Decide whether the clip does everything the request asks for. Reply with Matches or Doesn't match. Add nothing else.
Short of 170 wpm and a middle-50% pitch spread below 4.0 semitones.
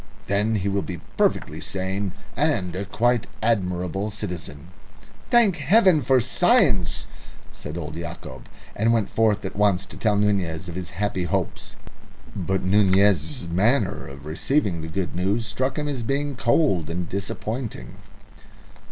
Doesn't match